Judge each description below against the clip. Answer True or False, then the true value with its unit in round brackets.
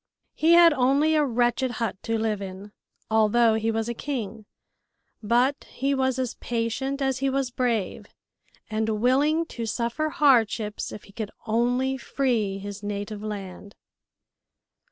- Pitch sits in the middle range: False (235 Hz)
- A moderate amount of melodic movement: True (3.7 semitones)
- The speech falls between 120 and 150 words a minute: True (145 wpm)